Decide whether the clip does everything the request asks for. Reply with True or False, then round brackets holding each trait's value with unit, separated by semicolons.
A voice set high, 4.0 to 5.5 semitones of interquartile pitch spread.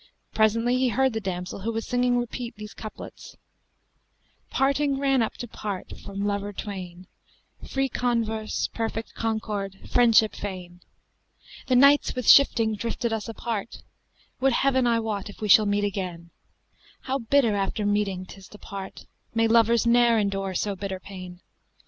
False (220 Hz; 3.3 semitones)